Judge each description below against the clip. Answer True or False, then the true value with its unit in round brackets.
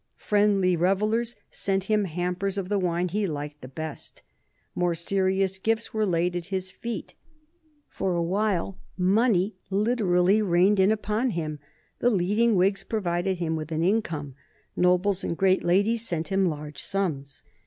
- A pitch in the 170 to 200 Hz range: True (190 Hz)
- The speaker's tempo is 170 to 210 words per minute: False (155 wpm)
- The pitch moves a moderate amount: True (3.1 semitones)